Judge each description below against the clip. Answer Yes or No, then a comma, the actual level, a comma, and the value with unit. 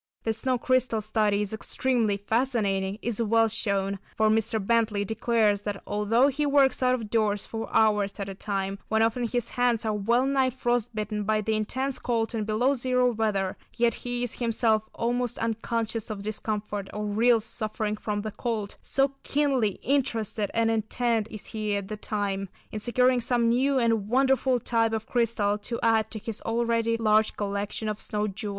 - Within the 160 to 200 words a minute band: Yes, average, 180 wpm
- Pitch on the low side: No, high, 225 Hz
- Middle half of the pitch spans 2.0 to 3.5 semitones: Yes, narrow, 2.4 semitones